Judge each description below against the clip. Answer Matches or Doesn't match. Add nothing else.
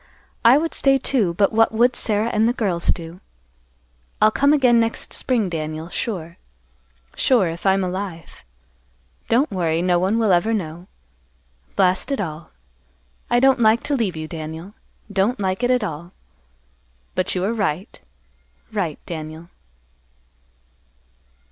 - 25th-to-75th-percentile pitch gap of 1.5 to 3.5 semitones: Doesn't match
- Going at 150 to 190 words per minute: Doesn't match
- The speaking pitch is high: Matches